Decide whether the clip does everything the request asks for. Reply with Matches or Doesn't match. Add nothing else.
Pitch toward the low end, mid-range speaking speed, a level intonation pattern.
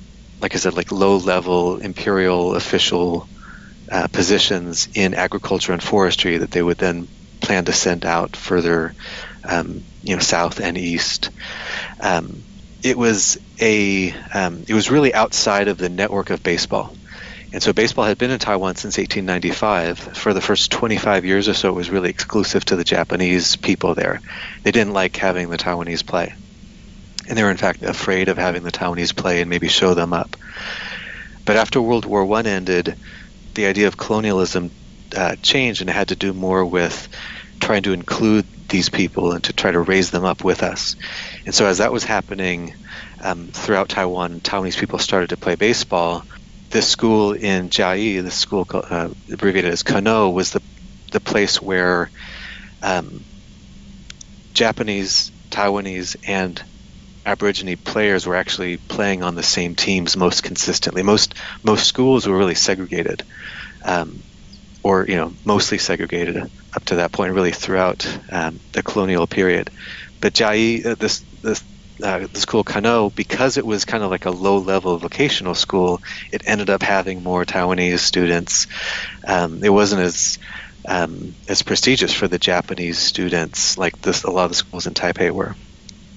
Matches